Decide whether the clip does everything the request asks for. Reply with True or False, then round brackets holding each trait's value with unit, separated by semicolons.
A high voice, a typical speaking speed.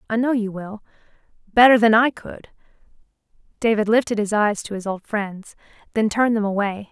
True (215 Hz; 175 wpm)